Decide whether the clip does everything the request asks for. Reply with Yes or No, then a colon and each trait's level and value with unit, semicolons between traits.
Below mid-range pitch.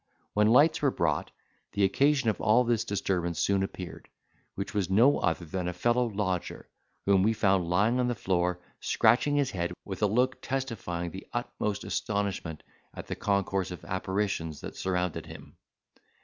Yes: low, 100 Hz